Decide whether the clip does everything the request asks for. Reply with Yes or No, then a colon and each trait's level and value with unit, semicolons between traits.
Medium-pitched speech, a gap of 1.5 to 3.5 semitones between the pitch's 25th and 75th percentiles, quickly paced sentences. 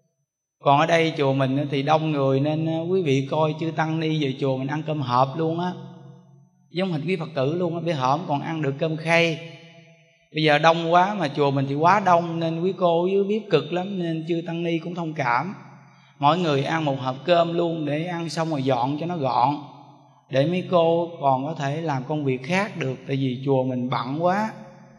No: medium, 160 Hz; average, 3.1 semitones; average, 225 wpm